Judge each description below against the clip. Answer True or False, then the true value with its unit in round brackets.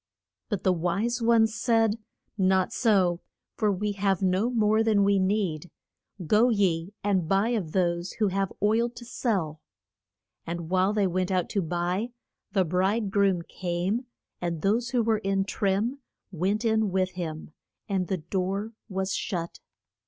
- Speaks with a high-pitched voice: True (195 Hz)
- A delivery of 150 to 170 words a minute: True (155 wpm)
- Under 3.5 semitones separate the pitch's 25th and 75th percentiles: True (3.1 semitones)